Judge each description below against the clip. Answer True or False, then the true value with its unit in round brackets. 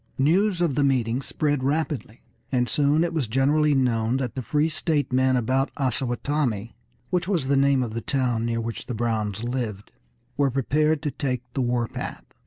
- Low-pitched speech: True (130 Hz)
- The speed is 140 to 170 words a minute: False (185 wpm)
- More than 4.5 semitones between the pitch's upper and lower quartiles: False (3.6 semitones)